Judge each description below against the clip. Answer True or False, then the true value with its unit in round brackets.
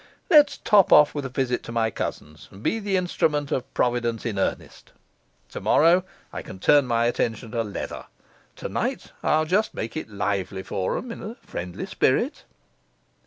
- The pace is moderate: True (165 wpm)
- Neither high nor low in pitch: False (125 Hz)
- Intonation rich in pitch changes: True (6.8 semitones)